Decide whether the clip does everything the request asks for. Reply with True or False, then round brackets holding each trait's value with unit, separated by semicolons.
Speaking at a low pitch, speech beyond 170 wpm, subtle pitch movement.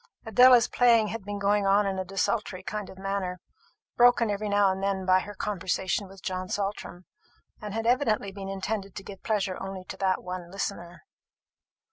False (195 Hz; 180 wpm; 1.8 semitones)